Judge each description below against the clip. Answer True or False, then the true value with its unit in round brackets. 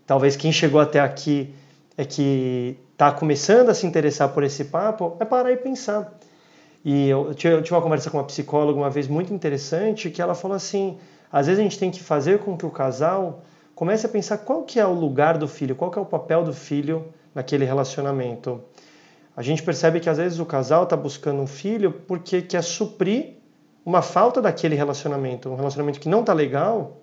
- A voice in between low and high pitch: True (160 Hz)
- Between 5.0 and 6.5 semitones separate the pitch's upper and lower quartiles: False (4.4 semitones)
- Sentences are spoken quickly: True (200 wpm)